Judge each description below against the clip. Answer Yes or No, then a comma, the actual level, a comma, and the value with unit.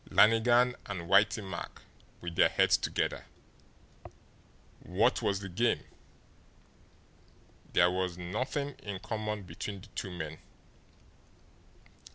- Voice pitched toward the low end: Yes, low, 100 Hz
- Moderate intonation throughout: Yes, average, 3.6 semitones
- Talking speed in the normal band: No, slow, 105 wpm